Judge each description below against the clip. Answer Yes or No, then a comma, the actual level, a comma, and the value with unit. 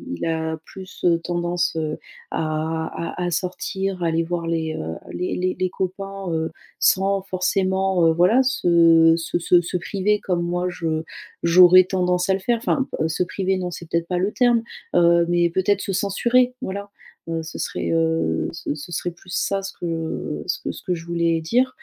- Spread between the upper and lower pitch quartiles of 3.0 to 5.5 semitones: No, narrow, 2.5 semitones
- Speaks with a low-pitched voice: No, medium, 175 Hz